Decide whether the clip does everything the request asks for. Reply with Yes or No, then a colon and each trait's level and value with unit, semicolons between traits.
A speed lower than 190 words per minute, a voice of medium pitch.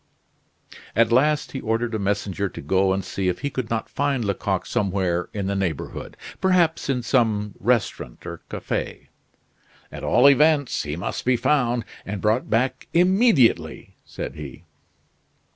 No: average, 150 wpm; low, 115 Hz